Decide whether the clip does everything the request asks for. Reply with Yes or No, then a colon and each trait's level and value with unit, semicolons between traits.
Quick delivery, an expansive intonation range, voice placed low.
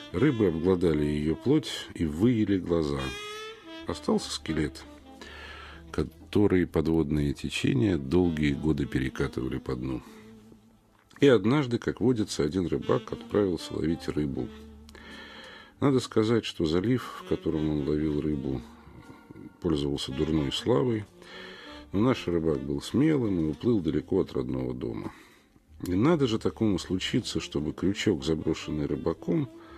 No: average, 115 wpm; wide, 6.8 semitones; very low, 80 Hz